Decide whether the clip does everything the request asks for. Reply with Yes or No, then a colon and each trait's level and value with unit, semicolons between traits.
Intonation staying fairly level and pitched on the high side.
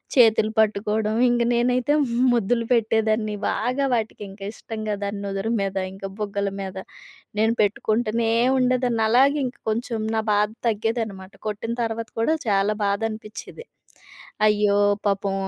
Yes: narrow, 2.2 semitones; high, 220 Hz